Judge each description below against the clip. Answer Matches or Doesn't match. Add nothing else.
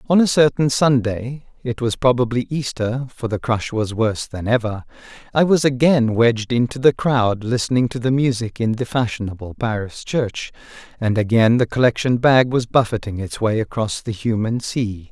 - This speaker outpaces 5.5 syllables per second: Doesn't match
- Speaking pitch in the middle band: Doesn't match